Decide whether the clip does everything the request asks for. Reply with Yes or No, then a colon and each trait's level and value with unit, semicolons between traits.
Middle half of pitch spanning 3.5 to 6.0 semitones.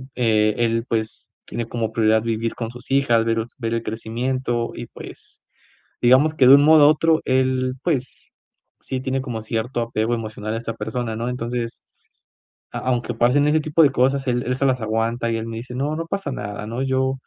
No: narrow, 2.6 semitones